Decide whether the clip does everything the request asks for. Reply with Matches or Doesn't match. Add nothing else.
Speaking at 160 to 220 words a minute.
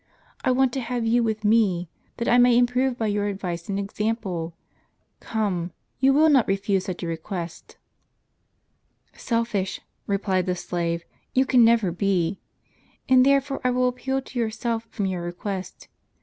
Matches